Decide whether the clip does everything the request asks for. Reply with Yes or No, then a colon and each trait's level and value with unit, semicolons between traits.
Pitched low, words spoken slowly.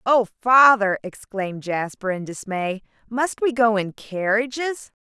No: high, 220 Hz; slow, 130 wpm